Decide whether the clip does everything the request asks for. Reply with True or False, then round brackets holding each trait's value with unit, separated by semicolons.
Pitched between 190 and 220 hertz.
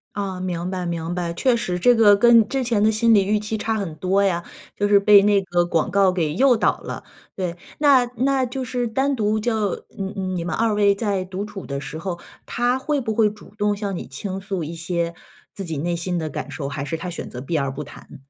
True (195 Hz)